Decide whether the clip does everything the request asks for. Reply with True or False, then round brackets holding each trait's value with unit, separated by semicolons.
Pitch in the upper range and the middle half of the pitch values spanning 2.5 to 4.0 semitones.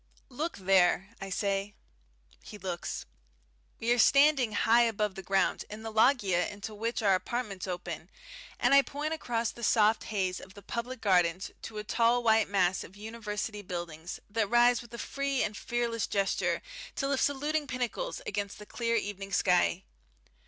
True (215 Hz; 3.7 semitones)